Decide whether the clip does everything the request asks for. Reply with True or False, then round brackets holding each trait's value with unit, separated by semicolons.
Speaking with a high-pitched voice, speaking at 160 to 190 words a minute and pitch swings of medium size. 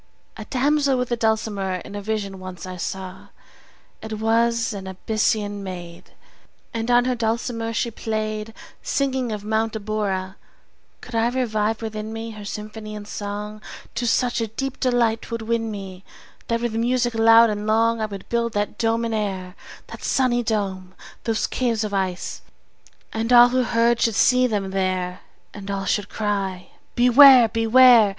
False (220 Hz; 170 wpm; 2.3 semitones)